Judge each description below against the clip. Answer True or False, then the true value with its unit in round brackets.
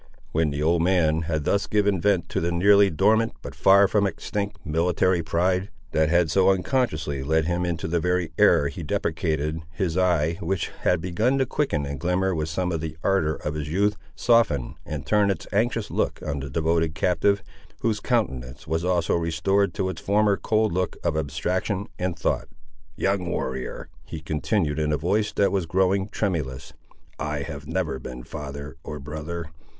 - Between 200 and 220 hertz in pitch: False (85 Hz)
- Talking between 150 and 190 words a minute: True (180 wpm)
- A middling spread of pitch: True (4.0 semitones)